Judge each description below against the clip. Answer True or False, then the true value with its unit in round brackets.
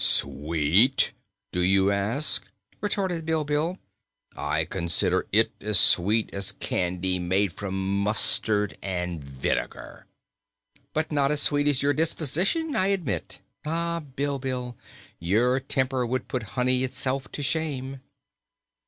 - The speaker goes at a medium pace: False (120 wpm)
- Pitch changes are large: True (7.2 semitones)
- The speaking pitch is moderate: False (125 Hz)